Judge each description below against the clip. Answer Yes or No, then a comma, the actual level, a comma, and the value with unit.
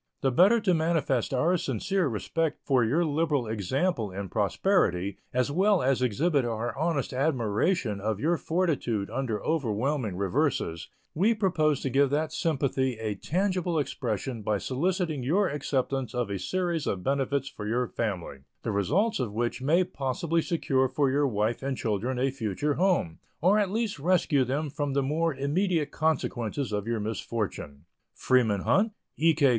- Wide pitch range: Yes, wide, 6.3 semitones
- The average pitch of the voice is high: No, low, 135 Hz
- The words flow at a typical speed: Yes, average, 160 wpm